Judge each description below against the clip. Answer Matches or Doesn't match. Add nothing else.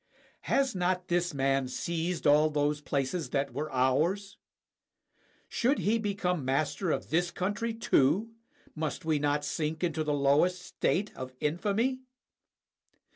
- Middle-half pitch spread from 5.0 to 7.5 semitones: Doesn't match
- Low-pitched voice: Doesn't match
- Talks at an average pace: Doesn't match